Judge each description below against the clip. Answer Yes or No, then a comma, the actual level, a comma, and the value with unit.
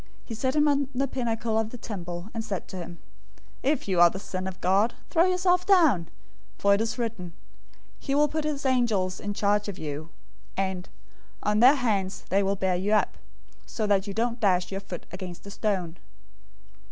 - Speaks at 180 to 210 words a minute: Yes, average, 195 wpm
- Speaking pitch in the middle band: No, high, 210 Hz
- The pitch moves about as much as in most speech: Yes, average, 4.9 semitones